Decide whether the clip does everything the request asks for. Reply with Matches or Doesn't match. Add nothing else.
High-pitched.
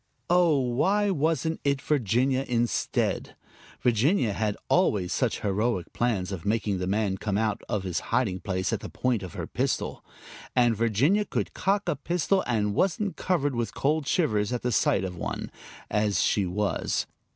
Doesn't match